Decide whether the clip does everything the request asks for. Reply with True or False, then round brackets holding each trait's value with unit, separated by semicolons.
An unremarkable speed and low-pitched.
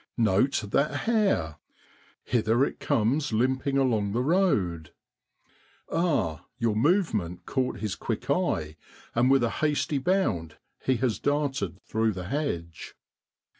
False (125 wpm; 120 Hz)